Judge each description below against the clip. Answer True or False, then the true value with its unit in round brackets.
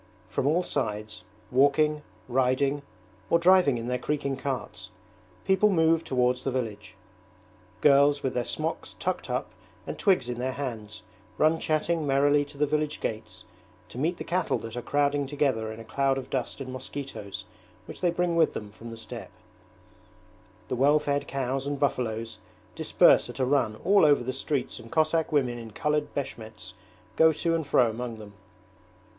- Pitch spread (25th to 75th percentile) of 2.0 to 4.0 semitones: True (3.7 semitones)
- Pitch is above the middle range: False (140 Hz)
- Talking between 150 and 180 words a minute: True (170 wpm)